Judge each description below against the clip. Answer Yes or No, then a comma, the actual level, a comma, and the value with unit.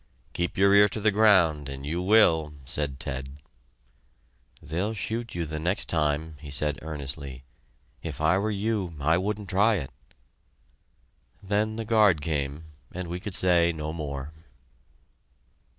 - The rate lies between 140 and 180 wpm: Yes, average, 145 wpm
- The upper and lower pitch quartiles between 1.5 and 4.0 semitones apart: No, average, 5.3 semitones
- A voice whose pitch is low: Yes, very low, 85 Hz